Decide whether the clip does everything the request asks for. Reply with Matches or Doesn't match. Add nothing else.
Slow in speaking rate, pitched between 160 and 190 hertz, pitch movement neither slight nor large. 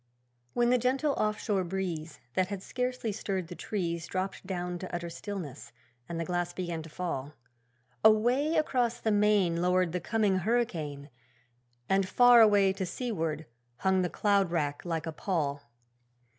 Doesn't match